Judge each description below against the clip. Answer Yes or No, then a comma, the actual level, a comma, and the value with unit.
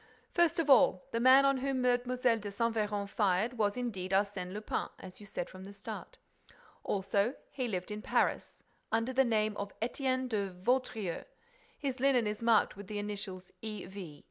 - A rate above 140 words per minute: Yes, average, 180 wpm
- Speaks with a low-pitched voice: No, high, 215 Hz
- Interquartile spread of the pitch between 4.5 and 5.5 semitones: No, average, 4.0 semitones